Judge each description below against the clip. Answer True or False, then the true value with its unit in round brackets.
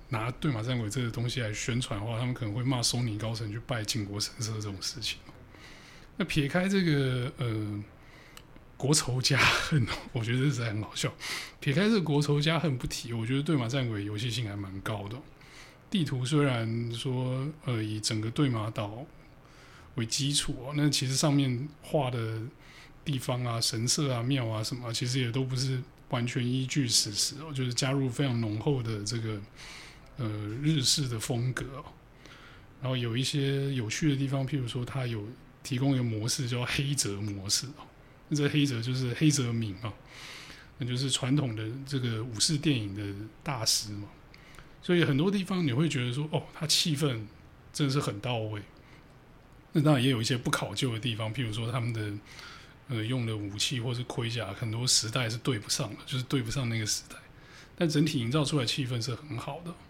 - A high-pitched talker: False (130 Hz)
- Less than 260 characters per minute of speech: False (275 characters per minute)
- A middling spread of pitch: True (4.0 semitones)